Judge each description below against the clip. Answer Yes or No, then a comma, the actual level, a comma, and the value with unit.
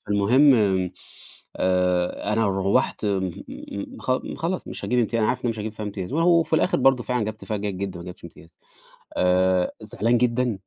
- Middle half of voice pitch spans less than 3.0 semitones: No, average, 4.8 semitones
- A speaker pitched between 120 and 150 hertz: No, low, 105 Hz